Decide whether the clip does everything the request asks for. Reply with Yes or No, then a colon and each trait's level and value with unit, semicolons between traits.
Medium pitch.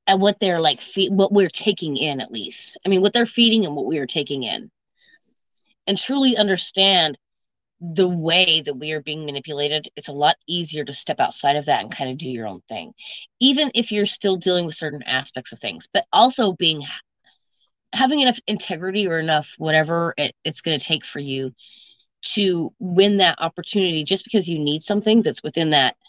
Yes: medium, 175 Hz